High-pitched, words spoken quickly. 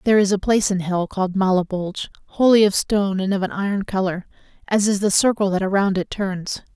Yes: high, 195 Hz; fast, 215 wpm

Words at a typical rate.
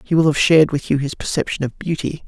No: fast, 265 wpm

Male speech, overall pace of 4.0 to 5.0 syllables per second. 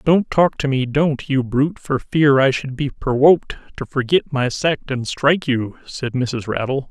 Yes: male; 4.5 syllables/s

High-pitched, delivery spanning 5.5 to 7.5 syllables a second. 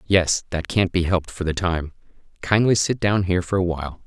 No: very low, 90 Hz; 5.6 syllables/s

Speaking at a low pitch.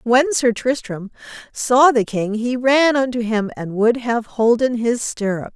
No: high, 235 Hz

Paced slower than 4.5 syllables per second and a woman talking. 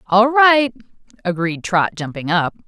Yes: 4.2 syllables/s; female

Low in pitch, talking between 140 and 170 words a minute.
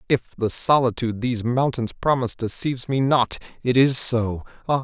Yes: low, 125 Hz; average, 160 wpm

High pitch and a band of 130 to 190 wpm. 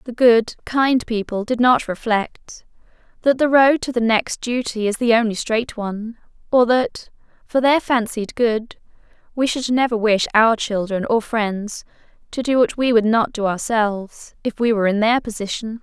Yes: high, 230 Hz; average, 180 wpm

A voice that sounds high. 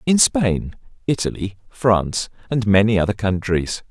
No: low, 105 Hz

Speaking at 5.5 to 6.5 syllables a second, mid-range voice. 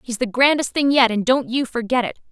No: 5.8 syllables/s; high, 245 Hz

